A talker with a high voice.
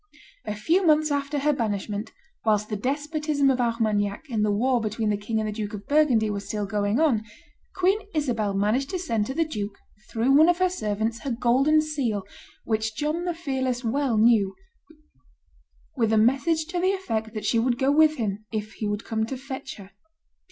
Yes: high, 235 Hz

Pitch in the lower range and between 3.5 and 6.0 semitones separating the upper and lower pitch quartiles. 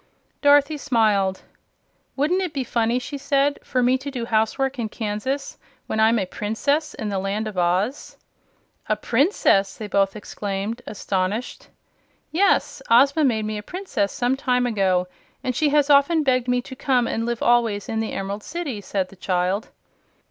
No: high, 235 Hz; average, 5.1 semitones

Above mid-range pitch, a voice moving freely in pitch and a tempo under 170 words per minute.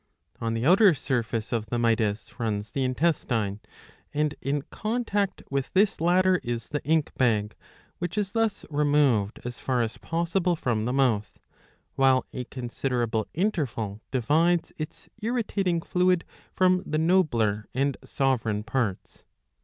No: low, 135 Hz; wide, 7.2 semitones; average, 140 wpm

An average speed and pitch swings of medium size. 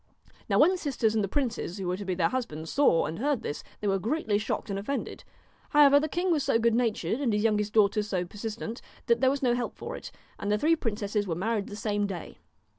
No: fast, 245 wpm; average, 4.6 semitones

